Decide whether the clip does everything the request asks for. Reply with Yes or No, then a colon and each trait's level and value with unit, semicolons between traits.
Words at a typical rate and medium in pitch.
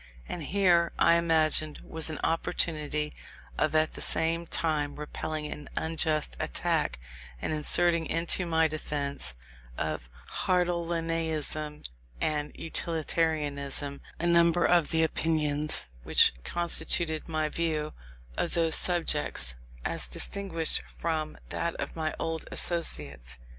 No: slow, 115 wpm; medium, 160 Hz